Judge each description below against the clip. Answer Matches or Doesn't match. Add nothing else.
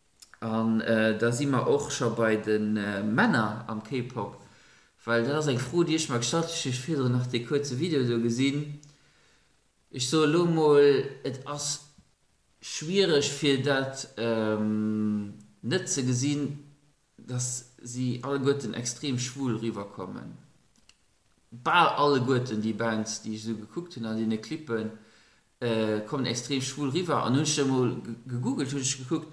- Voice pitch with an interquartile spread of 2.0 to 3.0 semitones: Doesn't match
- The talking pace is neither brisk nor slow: Doesn't match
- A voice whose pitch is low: Matches